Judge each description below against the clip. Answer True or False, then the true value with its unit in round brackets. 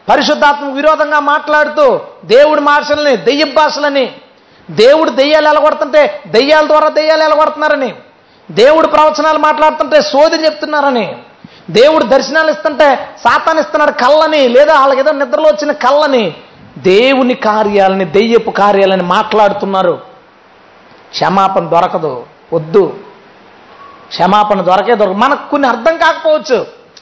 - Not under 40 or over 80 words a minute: False (100 wpm)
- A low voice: False (295 Hz)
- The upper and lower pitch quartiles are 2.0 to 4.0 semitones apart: False (4.6 semitones)